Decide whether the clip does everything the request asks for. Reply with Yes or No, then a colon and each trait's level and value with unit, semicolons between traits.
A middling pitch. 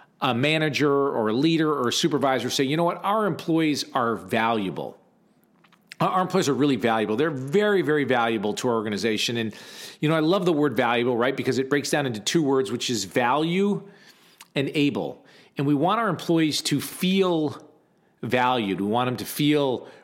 Yes: medium, 145 Hz